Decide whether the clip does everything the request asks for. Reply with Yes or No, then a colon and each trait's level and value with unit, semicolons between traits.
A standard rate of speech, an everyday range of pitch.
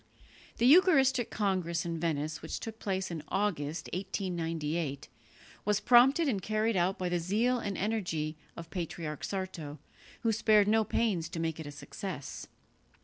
Yes: average, 150 wpm; average, 4.8 semitones